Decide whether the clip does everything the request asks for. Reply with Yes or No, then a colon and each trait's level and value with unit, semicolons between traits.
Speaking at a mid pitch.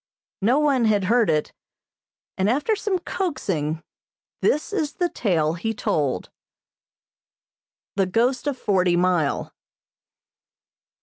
No: high, 215 Hz